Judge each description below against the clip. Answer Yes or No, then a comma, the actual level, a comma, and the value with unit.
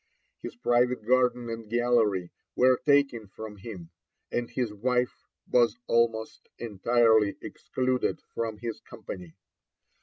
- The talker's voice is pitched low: Yes, low, 115 Hz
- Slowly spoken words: Yes, slow, 115 wpm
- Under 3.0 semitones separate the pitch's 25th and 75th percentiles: Yes, narrow, 2.4 semitones